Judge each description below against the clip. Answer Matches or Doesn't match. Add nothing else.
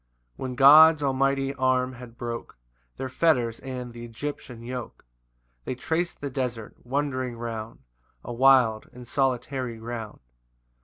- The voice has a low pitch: Matches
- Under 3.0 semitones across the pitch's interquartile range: Matches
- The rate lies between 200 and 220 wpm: Doesn't match